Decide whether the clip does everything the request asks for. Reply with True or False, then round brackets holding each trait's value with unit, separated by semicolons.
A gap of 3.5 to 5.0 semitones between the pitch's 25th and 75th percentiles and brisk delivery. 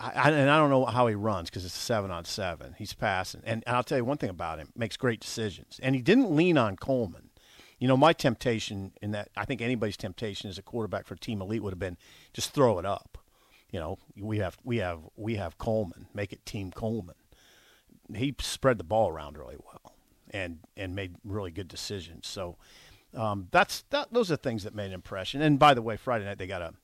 True (4.5 semitones; 230 wpm)